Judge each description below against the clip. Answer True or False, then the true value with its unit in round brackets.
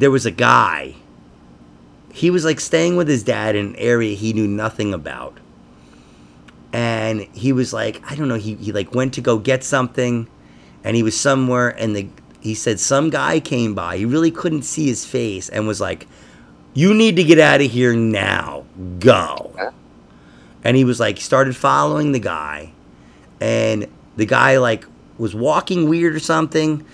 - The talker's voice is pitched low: True (110 Hz)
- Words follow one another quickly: False (180 wpm)